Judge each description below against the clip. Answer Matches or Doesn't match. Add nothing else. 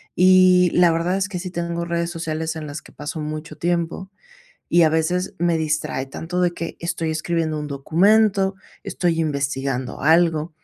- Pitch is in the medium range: Matches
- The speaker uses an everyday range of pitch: Doesn't match